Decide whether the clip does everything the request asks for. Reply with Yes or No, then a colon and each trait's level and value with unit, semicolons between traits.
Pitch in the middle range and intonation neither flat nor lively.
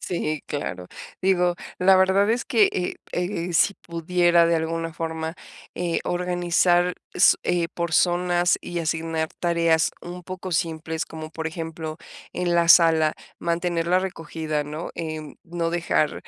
No: medium, 170 Hz; narrow, 1.7 semitones